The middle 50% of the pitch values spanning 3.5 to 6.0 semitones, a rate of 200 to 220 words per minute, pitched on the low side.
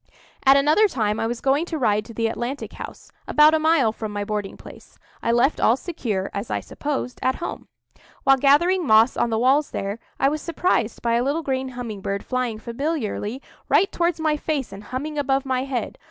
No: average, 5.0 semitones; fast, 205 wpm; very high, 260 Hz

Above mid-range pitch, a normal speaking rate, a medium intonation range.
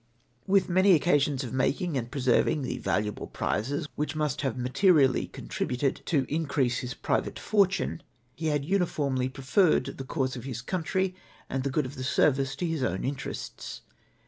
No: medium, 140 Hz; average, 170 wpm; average, 3.8 semitones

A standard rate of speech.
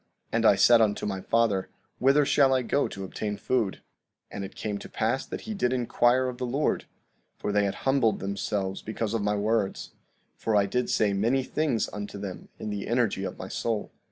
No: fast, 210 wpm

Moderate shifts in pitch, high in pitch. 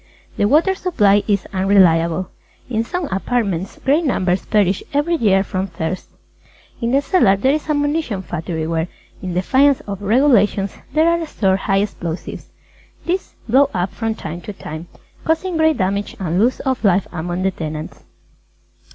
No: wide, 7.0 semitones; high, 200 Hz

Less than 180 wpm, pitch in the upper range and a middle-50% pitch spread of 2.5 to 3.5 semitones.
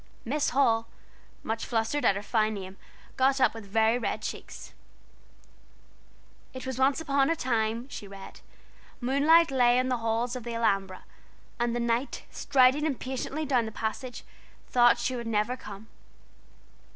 Yes: average, 150 wpm; high, 240 Hz; average, 2.9 semitones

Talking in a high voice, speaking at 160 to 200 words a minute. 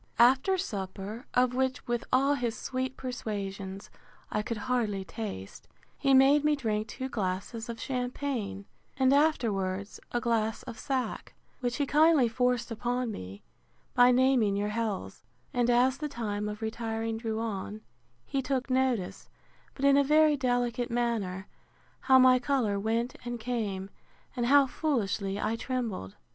No: high, 240 Hz; average, 150 wpm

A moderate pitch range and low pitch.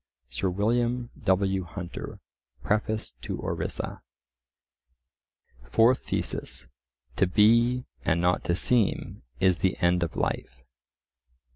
Yes: average, 4.6 semitones; very low, 95 Hz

